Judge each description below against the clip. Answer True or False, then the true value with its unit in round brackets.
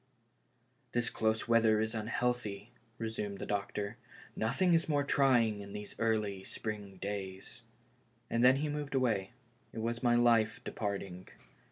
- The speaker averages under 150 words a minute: False (155 wpm)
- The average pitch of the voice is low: True (110 Hz)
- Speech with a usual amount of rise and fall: True (3.1 semitones)